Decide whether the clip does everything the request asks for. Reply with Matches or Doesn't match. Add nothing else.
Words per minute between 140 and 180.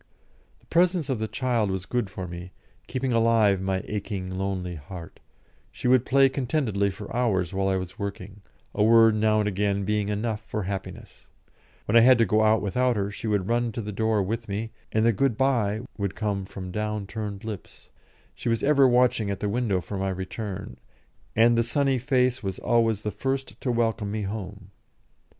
Doesn't match